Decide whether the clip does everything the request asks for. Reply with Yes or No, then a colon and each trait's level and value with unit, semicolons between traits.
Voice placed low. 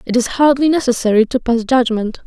No: high, 245 Hz